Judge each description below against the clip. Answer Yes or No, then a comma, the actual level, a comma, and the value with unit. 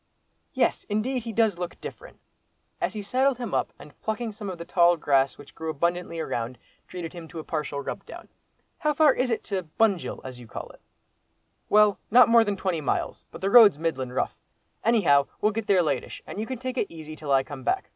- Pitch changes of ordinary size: No, wide, 6.4 semitones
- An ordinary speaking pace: No, fast, 215 wpm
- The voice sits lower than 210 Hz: Yes, medium, 185 Hz